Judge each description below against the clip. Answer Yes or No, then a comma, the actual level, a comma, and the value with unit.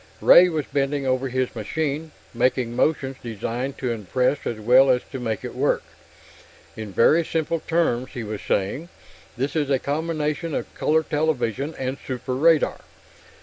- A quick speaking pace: No, average, 155 wpm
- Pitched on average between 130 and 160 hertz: Yes, low, 135 Hz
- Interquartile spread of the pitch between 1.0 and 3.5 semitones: No, average, 3.9 semitones